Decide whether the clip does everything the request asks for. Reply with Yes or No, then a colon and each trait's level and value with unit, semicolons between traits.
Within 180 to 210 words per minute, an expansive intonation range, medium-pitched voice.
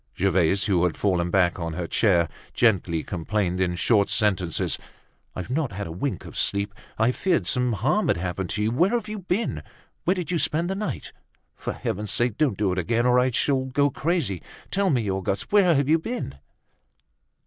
No: average, 195 wpm; wide, 8.2 semitones; low, 110 Hz